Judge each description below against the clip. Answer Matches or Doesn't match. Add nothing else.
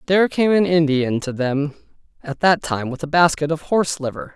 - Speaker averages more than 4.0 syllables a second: Matches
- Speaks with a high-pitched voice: Doesn't match